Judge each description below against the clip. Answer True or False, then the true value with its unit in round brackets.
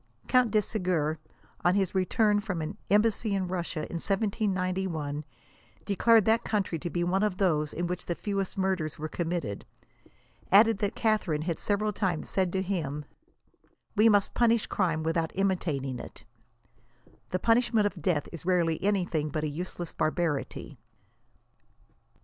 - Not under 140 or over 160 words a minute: True (155 wpm)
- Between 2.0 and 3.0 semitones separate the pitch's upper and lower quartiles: False (3.9 semitones)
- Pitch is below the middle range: False (185 Hz)